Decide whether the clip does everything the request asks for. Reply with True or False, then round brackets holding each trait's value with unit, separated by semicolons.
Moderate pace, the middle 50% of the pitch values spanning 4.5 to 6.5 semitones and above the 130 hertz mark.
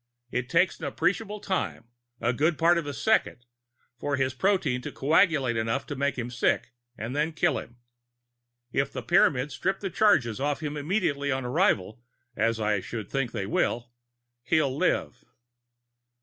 True (165 wpm; 5.3 semitones; 140 Hz)